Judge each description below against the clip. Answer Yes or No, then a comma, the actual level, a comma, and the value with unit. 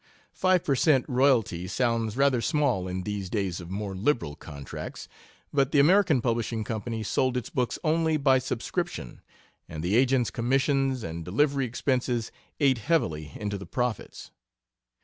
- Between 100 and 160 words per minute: Yes, average, 150 wpm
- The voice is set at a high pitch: No, low, 120 Hz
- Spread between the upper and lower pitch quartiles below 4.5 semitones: No, average, 5.1 semitones